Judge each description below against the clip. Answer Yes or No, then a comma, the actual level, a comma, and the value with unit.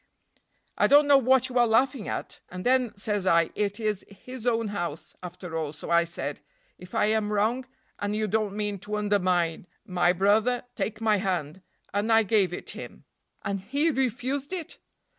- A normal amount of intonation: Yes, average, 4.6 semitones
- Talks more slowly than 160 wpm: No, average, 180 wpm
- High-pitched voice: Yes, high, 210 Hz